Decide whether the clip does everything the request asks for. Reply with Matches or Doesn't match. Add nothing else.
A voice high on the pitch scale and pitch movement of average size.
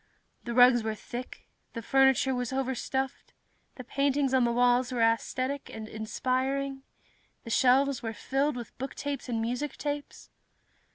Doesn't match